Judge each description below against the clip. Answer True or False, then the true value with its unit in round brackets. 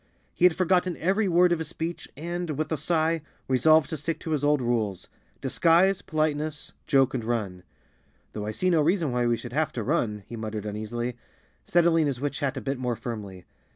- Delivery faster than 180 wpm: True (195 wpm)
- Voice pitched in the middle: True (145 Hz)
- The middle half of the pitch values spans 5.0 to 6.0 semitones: True (5.6 semitones)